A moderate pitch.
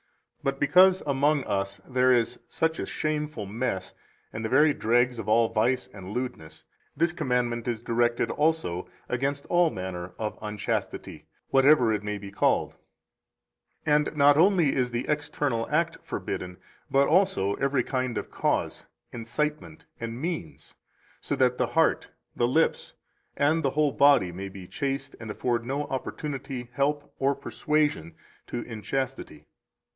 No: low, 130 Hz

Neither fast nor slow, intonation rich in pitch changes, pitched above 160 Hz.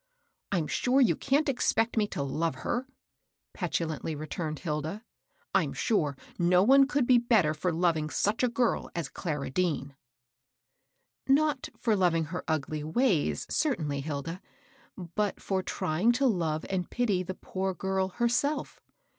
Yes: average, 155 wpm; wide, 7.3 semitones; medium, 185 Hz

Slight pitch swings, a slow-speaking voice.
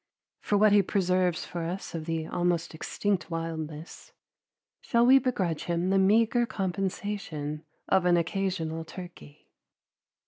No: average, 3.2 semitones; slow, 130 wpm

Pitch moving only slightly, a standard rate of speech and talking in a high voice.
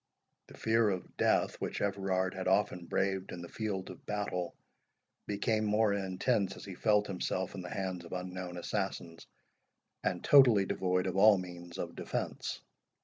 No: narrow, 2.2 semitones; average, 160 wpm; very low, 95 Hz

